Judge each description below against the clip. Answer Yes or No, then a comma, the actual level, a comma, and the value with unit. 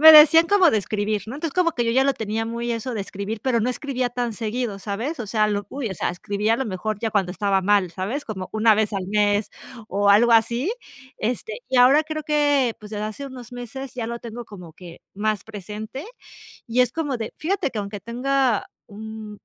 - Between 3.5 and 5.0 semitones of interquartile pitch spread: Yes, average, 3.9 semitones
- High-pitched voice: Yes, high, 225 Hz